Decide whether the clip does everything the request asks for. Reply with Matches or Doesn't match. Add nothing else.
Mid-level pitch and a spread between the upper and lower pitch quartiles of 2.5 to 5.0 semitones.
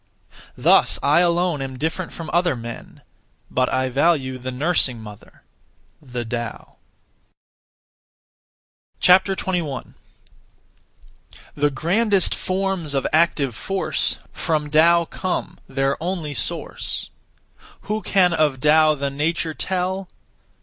Matches